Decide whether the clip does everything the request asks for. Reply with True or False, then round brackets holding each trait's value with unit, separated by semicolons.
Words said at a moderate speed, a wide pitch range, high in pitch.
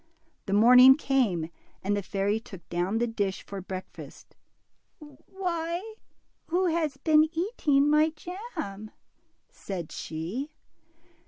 False (110 wpm; 8.4 semitones; 265 Hz)